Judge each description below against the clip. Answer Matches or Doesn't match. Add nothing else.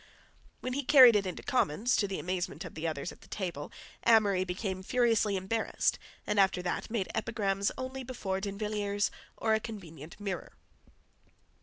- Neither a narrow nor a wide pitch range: Matches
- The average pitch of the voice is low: Doesn't match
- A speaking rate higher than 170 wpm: Doesn't match